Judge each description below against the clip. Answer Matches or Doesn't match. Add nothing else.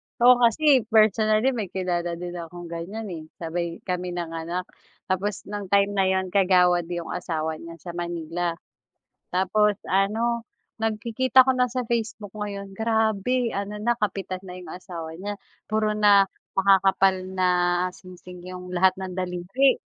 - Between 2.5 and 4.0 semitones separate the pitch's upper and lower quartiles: Matches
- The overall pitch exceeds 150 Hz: Matches